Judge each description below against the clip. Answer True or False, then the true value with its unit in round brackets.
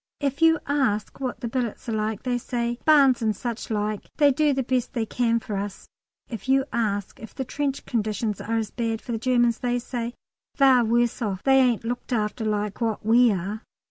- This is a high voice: True (235 Hz)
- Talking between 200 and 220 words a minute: True (205 wpm)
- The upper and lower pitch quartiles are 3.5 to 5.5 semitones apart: False (3.0 semitones)